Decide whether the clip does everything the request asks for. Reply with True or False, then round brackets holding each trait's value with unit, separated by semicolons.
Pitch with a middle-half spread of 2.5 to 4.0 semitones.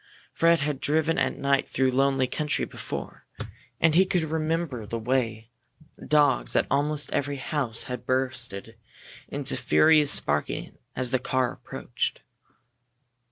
True (3.2 semitones)